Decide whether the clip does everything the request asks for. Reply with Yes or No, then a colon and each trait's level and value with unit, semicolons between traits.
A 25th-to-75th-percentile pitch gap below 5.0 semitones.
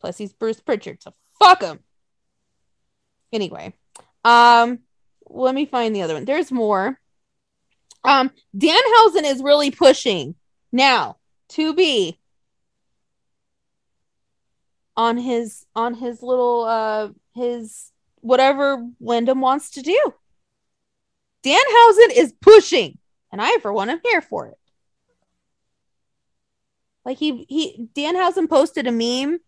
No: wide, 5.5 semitones